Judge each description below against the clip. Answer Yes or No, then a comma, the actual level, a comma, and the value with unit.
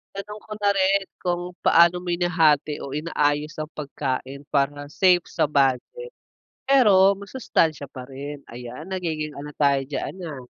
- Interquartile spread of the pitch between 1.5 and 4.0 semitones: No, average, 4.8 semitones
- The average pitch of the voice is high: No, medium, 155 Hz